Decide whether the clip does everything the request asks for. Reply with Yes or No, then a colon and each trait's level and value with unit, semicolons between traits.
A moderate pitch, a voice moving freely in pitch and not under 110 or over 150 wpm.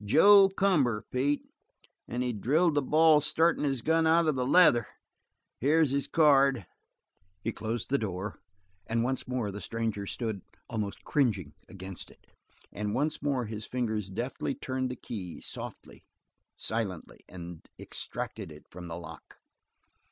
No: low, 125 Hz; wide, 5.7 semitones; average, 145 wpm